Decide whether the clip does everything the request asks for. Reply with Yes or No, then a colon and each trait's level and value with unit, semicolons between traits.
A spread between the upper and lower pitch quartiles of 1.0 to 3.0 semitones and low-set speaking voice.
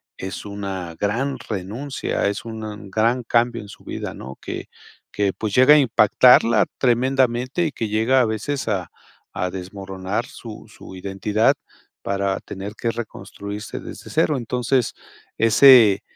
No: average, 3.9 semitones; low, 110 Hz